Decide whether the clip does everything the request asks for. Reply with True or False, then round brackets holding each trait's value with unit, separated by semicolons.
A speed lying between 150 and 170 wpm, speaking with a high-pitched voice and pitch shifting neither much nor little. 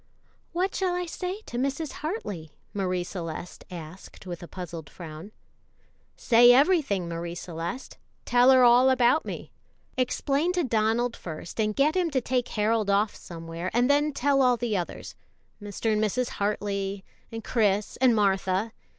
False (155 wpm; 225 Hz; 5.9 semitones)